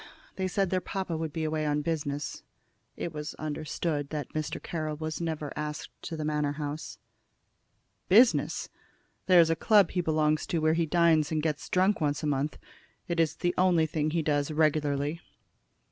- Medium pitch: Yes, medium, 155 Hz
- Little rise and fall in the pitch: Yes, narrow, 2.1 semitones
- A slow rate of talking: No, average, 175 wpm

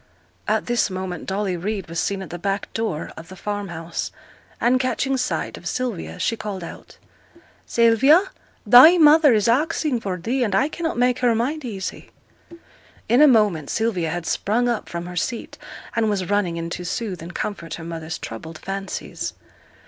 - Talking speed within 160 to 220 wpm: Yes, average, 175 wpm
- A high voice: Yes, high, 205 Hz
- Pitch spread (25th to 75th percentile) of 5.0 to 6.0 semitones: Yes, wide, 5.5 semitones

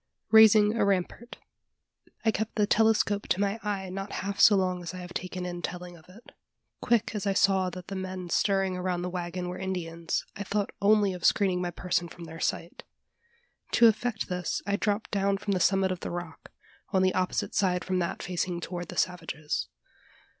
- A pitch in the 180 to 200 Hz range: Yes, medium, 185 Hz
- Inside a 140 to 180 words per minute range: No, average, 195 wpm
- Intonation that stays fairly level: Yes, narrow, 2.1 semitones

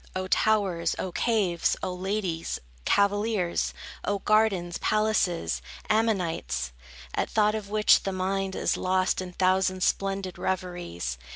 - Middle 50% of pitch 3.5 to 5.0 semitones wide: No, average, 2.7 semitones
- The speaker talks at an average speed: No, slow, 120 wpm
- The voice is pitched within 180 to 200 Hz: Yes, high, 190 Hz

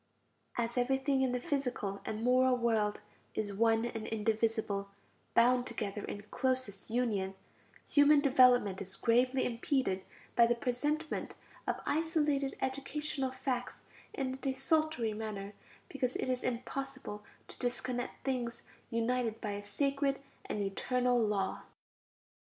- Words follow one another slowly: Yes, slow, 125 wpm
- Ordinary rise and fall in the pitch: Yes, average, 3.4 semitones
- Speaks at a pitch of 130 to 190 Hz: No, high, 245 Hz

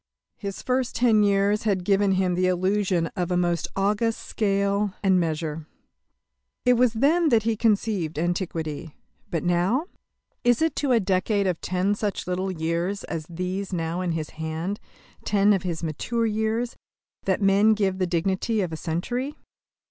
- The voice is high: Yes, high, 195 Hz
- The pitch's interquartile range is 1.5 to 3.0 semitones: No, average, 3.6 semitones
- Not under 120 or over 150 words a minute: No, average, 165 wpm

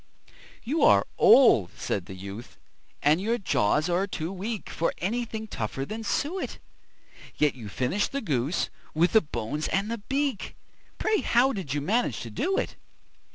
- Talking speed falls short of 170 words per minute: Yes, average, 160 wpm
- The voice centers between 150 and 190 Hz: Yes, medium, 185 Hz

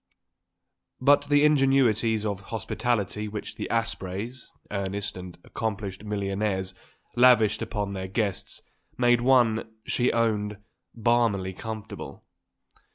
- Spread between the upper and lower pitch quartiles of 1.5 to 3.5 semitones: Yes, average, 3.1 semitones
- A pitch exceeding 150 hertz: No, low, 110 Hz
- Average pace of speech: No, slow, 100 wpm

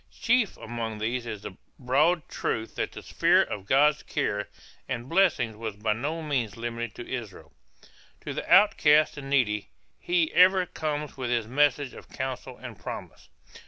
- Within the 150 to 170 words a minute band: Yes, average, 160 wpm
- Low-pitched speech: Yes, low, 130 Hz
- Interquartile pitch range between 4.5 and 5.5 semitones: Yes, average, 4.8 semitones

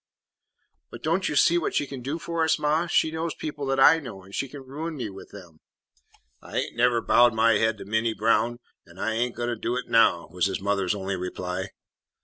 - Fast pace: Yes, fast, 230 wpm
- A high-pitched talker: No, low, 120 Hz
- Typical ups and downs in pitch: No, wide, 6.5 semitones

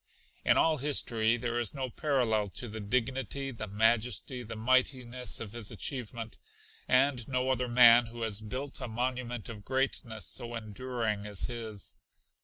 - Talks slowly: No, average, 155 wpm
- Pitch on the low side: Yes, low, 120 Hz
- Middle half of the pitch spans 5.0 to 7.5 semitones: No, narrow, 2.5 semitones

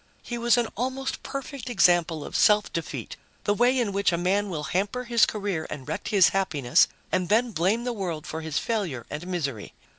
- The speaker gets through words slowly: No, average, 200 wpm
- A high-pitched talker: Yes, high, 195 Hz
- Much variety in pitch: Yes, wide, 6.1 semitones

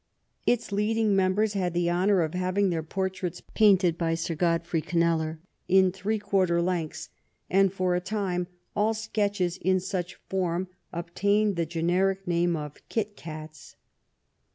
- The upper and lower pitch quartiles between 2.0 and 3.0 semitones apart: Yes, average, 2.7 semitones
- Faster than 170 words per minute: No, average, 155 wpm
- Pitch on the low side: No, medium, 180 Hz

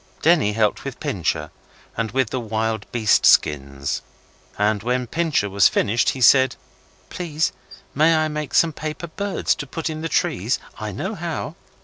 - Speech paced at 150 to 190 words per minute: Yes, average, 160 wpm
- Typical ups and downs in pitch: No, wide, 6.4 semitones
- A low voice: Yes, low, 130 Hz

